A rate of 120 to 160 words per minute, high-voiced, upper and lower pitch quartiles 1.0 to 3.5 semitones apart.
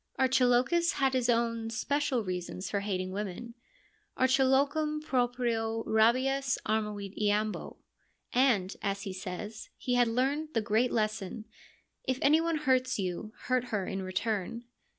No: average, 150 wpm; high, 235 Hz; average, 4.0 semitones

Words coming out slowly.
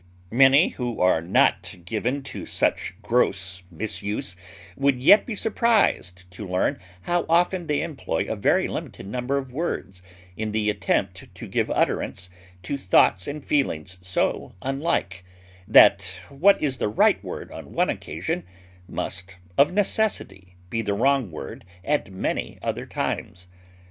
No: average, 145 wpm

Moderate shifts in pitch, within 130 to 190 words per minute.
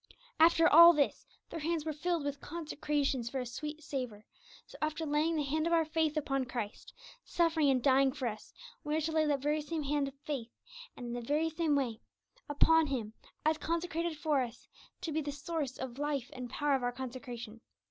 No: average, 3.4 semitones; fast, 205 wpm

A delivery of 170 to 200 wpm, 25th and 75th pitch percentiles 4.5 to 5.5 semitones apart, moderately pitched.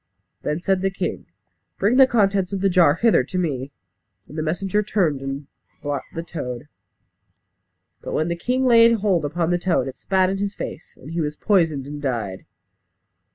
Yes: average, 185 wpm; average, 5.1 semitones; medium, 175 Hz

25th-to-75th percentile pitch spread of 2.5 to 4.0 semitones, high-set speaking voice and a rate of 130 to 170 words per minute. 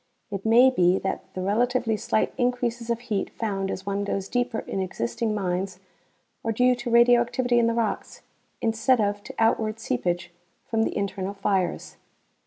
Yes: average, 3.4 semitones; high, 220 Hz; average, 165 wpm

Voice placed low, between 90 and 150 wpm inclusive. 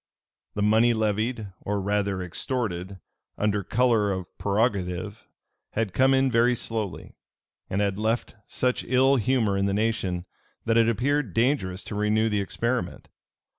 Yes: low, 110 Hz; average, 140 wpm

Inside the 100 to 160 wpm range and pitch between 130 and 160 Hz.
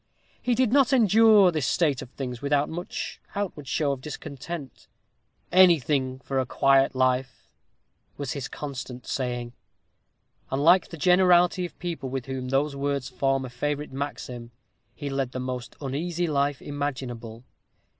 Yes: average, 145 wpm; medium, 140 Hz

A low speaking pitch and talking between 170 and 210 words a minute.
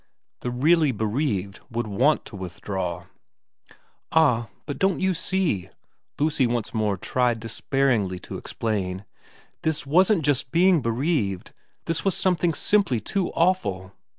No: low, 125 Hz; slow, 135 wpm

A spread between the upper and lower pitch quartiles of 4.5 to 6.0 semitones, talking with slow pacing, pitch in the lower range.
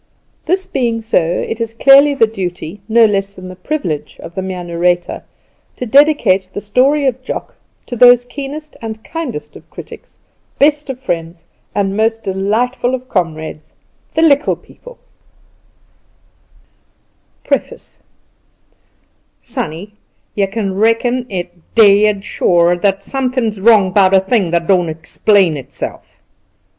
No: wide, 5.5 semitones; slow, 130 wpm; high, 210 Hz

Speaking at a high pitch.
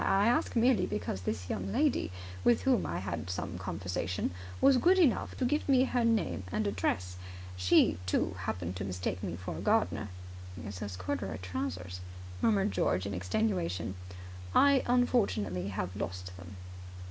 No: very low, 95 Hz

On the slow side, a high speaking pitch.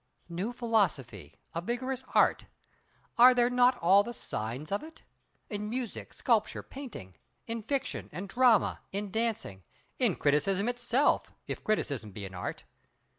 Yes: slow, 130 wpm; high, 215 Hz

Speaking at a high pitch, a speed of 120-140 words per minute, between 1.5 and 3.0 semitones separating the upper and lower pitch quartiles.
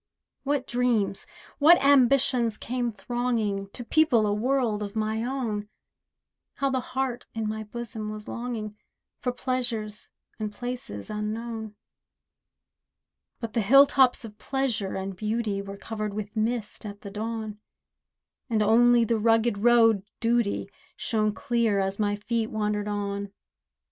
Yes: high, 225 Hz; slow, 135 wpm; narrow, 2.6 semitones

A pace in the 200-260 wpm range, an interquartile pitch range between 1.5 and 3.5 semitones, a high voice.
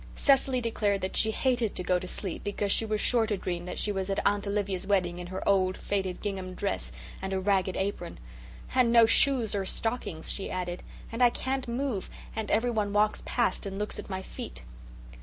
Yes: fast, 205 wpm; average, 3.2 semitones; high, 200 Hz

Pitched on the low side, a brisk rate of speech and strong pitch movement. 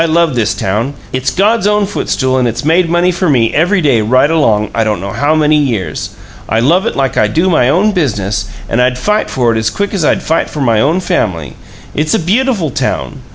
No: medium, 145 Hz; fast, 230 wpm; wide, 7.2 semitones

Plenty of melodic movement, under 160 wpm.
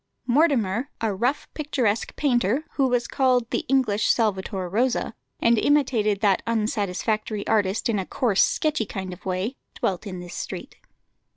No: average, 4.4 semitones; average, 150 wpm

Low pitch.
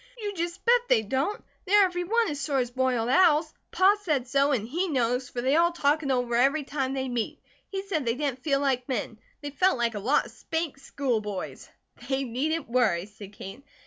No: very high, 275 Hz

